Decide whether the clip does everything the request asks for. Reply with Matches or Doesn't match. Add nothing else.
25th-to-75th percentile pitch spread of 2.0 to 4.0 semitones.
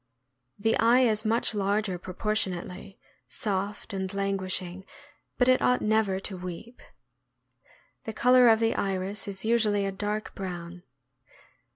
Matches